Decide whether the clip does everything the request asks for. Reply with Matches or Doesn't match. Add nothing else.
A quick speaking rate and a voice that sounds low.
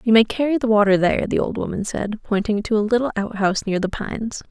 Doesn't match